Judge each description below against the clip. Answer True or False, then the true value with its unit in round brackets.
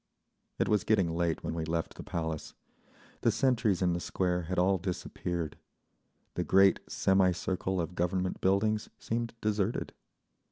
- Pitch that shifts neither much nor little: False (2.3 semitones)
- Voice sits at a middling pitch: False (95 Hz)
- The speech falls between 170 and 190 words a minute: False (150 wpm)